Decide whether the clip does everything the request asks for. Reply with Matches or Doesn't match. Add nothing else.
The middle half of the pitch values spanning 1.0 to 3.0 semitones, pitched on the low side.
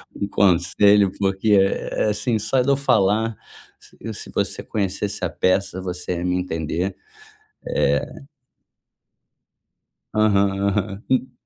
Matches